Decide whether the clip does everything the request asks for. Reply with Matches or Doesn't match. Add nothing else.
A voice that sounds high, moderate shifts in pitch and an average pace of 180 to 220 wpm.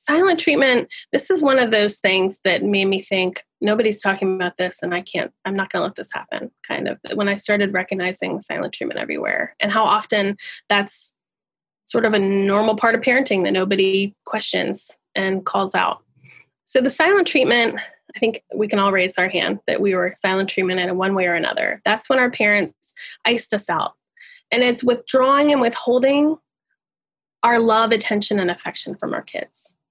Matches